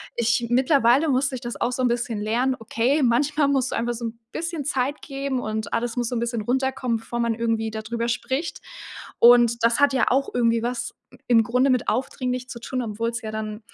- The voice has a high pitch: Yes, high, 240 Hz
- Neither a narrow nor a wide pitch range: No, narrow, 2.2 semitones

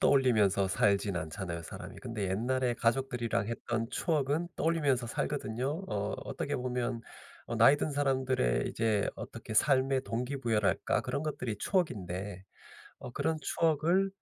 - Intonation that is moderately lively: Yes, average, 4.9 semitones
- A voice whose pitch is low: Yes, low, 125 Hz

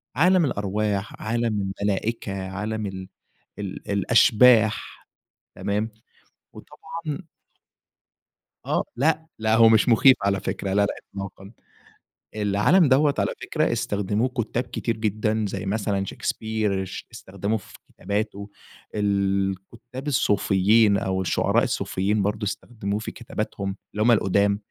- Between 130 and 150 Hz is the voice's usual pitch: No, low, 105 Hz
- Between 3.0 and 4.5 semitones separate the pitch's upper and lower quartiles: No, narrow, 2.5 semitones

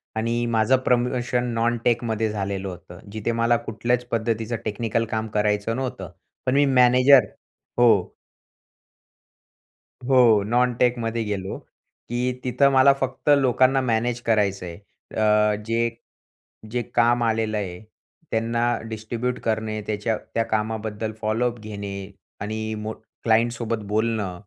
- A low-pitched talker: Yes, low, 115 Hz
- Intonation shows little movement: Yes, narrow, 2.1 semitones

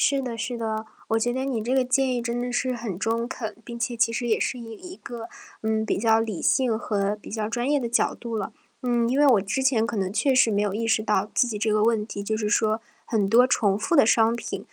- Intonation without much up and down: Yes, narrow, 2.2 semitones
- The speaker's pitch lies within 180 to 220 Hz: No, high, 230 Hz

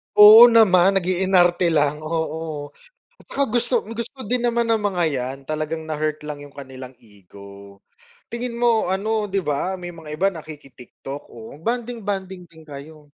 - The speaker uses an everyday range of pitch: No, wide, 6.0 semitones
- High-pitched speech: No, medium, 175 Hz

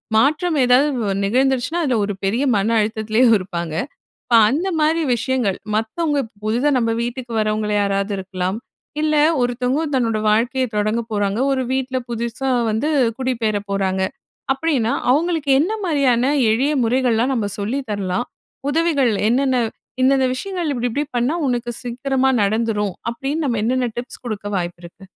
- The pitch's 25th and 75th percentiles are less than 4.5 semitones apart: Yes, average, 4.0 semitones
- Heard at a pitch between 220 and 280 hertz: Yes, high, 245 Hz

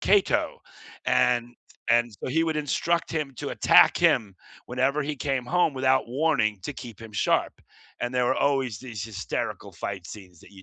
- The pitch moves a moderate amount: Yes, average, 4.8 semitones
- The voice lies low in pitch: Yes, low, 125 Hz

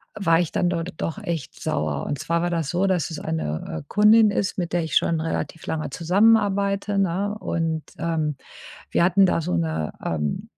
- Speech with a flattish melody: No, average, 4.1 semitones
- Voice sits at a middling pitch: Yes, medium, 170 Hz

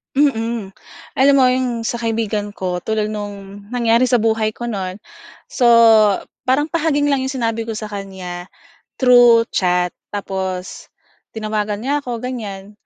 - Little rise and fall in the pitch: No, average, 3.6 semitones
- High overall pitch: Yes, high, 225 Hz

